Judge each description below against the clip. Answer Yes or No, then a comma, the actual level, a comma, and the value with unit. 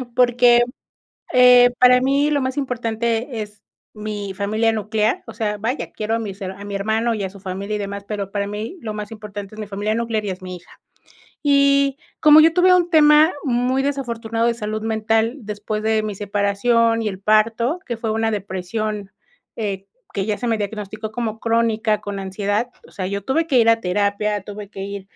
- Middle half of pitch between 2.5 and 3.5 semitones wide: Yes, average, 2.8 semitones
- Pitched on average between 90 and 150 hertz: No, high, 220 Hz